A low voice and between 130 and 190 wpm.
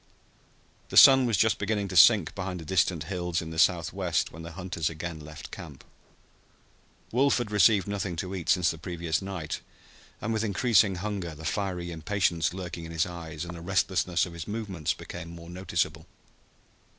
Yes: very low, 90 Hz; average, 175 wpm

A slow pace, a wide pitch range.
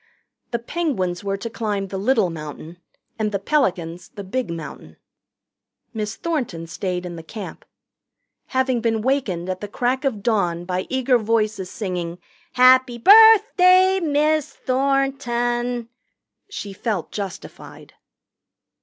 Yes: slow, 120 wpm; wide, 6.0 semitones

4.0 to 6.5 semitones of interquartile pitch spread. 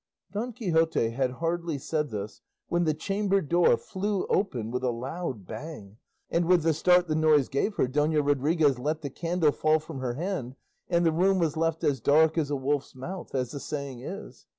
Yes: average, 4.4 semitones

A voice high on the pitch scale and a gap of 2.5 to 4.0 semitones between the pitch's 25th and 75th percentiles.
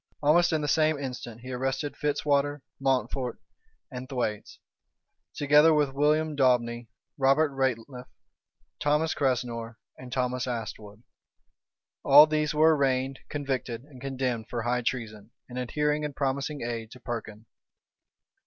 No: low, 135 Hz; average, 3.2 semitones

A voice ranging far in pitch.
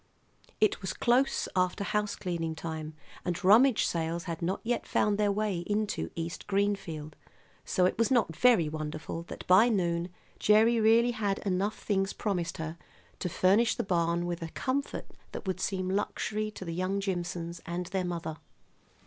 No: average, 3.7 semitones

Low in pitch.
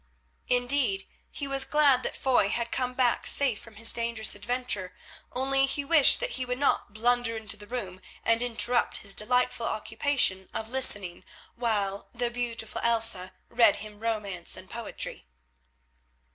No: high, 235 Hz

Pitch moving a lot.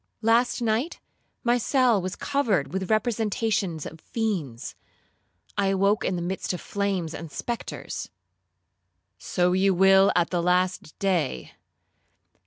No: average, 3.8 semitones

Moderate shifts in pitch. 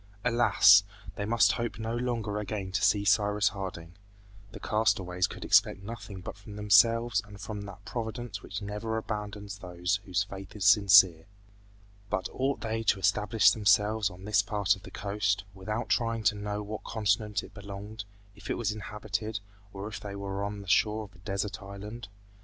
No: narrow, 1.7 semitones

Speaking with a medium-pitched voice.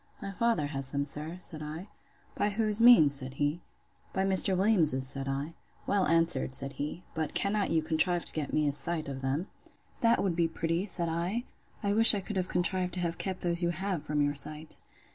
Yes: medium, 170 Hz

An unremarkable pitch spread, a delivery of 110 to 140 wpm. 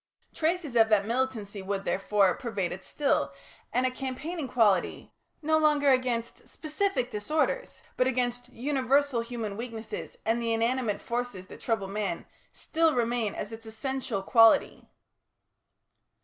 Yes: average, 3.6 semitones; slow, 135 wpm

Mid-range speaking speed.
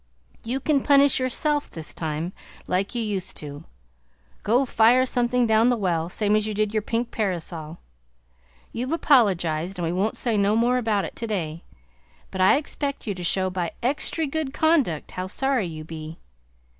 Yes: average, 170 wpm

